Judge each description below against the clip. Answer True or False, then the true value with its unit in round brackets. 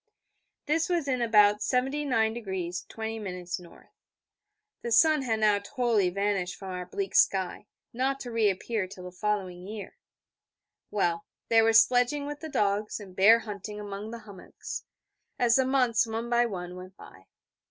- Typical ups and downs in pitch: True (3.8 semitones)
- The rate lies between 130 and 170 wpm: True (150 wpm)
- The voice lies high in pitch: True (215 Hz)